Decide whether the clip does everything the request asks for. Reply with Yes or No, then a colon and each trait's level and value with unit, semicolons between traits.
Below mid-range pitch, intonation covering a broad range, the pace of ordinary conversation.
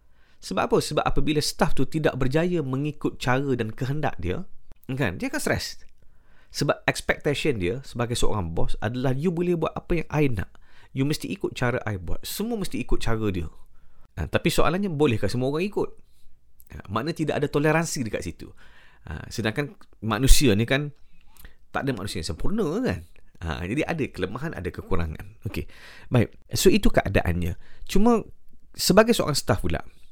Yes: low, 125 Hz; wide, 7.9 semitones; average, 165 wpm